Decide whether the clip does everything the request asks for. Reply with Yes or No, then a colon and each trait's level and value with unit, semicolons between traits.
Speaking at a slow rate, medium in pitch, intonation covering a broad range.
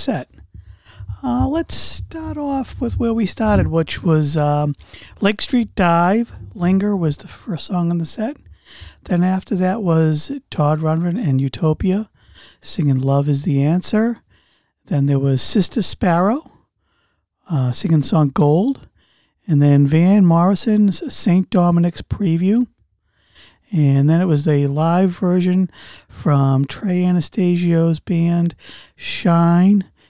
No: slow, 130 wpm; medium, 170 Hz; average, 4.8 semitones